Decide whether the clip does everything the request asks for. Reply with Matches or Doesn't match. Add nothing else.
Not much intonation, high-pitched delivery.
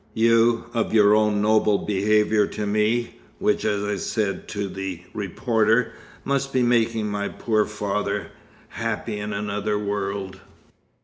Doesn't match